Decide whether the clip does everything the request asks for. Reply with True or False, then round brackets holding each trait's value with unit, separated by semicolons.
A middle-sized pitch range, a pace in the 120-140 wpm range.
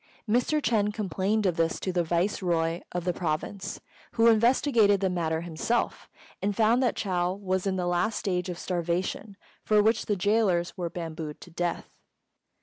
False (3.4 semitones; 165 wpm)